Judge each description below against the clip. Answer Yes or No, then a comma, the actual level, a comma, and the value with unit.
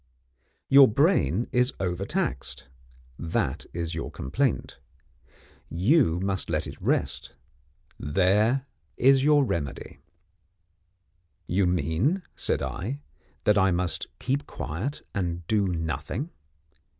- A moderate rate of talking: No, slow, 105 wpm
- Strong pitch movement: Yes, wide, 7.8 semitones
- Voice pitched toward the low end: Yes, very low, 95 Hz